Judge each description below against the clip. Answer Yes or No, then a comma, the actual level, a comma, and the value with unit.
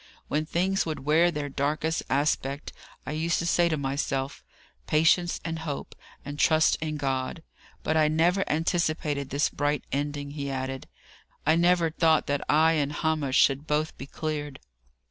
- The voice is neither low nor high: Yes, medium, 150 Hz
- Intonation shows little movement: Yes, narrow, 2.2 semitones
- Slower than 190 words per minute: Yes, average, 160 wpm